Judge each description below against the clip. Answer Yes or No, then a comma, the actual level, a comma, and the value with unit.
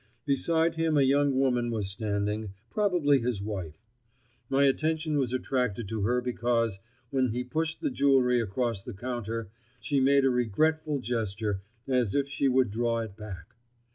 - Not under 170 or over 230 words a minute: No, average, 155 wpm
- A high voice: No, low, 125 Hz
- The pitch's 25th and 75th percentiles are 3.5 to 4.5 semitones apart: Yes, average, 4.2 semitones